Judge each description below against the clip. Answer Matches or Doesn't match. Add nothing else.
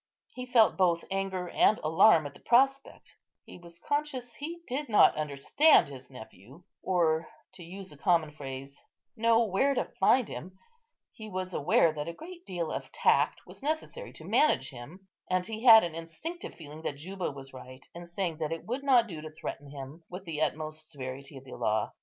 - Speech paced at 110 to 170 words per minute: Doesn't match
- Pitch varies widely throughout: Matches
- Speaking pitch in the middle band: Matches